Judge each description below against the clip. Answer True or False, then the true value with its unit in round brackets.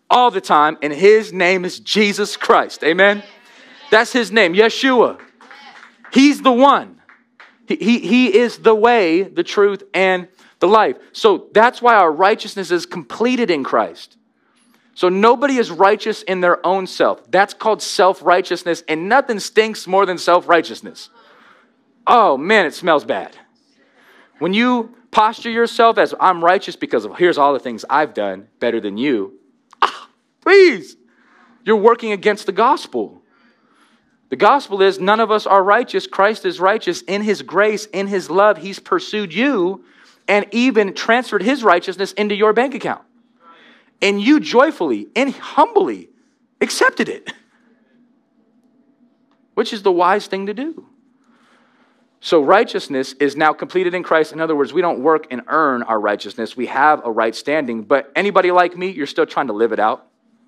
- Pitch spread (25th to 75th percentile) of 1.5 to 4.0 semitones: False (5.3 semitones)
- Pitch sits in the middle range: False (210 Hz)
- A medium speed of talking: True (160 wpm)